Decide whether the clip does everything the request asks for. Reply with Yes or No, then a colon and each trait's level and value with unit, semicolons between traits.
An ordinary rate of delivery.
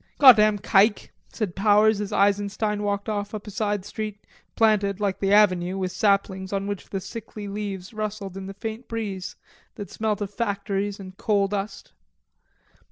Yes: average, 165 wpm